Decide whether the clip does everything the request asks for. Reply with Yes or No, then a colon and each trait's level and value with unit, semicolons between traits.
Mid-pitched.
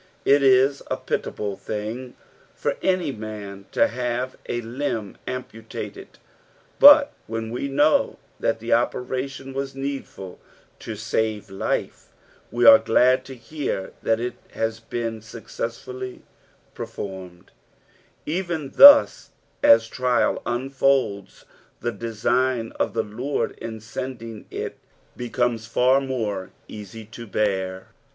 No: low, 120 Hz